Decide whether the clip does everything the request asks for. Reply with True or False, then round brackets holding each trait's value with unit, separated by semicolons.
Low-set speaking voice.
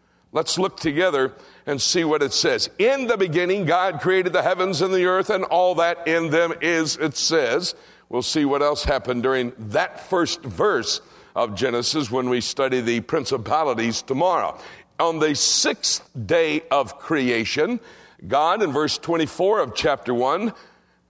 False (160 Hz)